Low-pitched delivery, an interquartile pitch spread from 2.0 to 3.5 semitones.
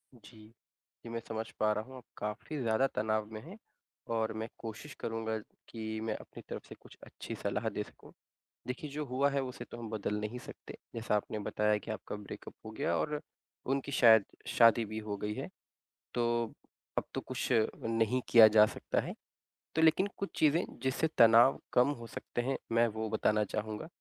Yes: low, 115 Hz; average, 2.9 semitones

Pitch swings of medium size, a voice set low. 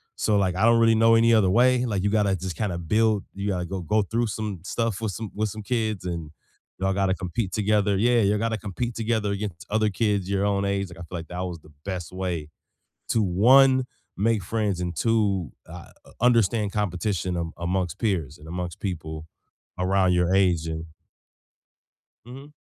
Yes: average, 3.5 semitones; low, 100 Hz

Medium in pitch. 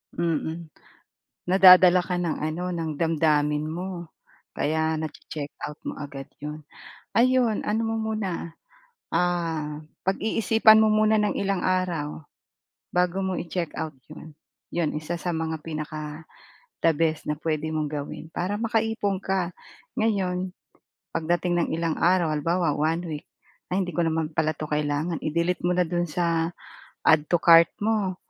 Yes: medium, 170 Hz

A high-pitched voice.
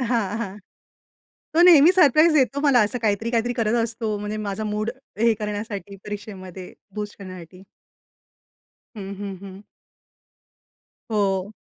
Yes: high, 210 Hz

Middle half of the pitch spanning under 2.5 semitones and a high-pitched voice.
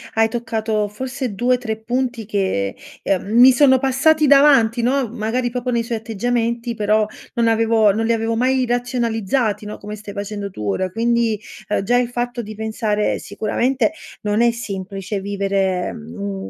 No: average, 2.9 semitones; high, 225 Hz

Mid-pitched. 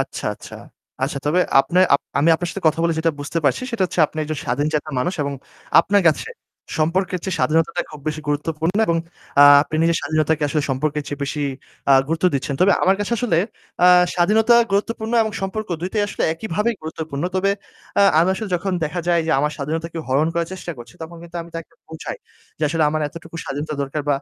Yes: medium, 165 Hz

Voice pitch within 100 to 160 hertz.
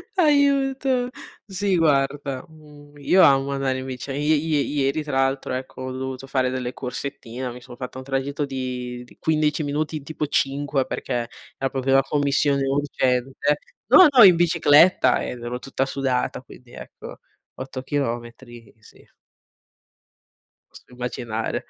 Yes: low, 135 Hz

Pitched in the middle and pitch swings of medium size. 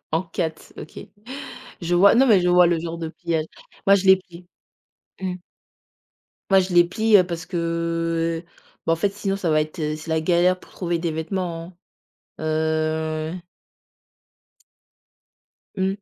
No: medium, 170 Hz; narrow, 2.3 semitones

